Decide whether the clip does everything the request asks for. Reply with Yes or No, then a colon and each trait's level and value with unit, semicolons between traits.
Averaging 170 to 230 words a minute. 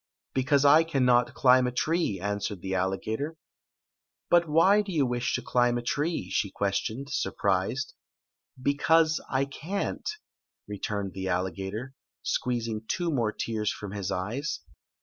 No: average, 150 wpm